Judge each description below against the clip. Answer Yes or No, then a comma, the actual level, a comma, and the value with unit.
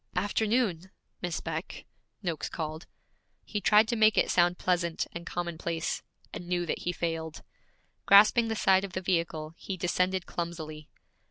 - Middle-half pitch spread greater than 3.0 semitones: No, average, 2.7 semitones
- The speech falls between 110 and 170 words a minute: Yes, average, 150 wpm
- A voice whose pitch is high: No, medium, 175 Hz